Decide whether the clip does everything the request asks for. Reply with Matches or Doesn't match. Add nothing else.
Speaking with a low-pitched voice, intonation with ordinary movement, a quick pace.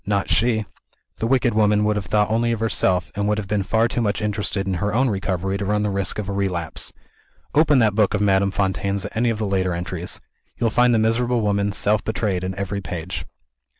Doesn't match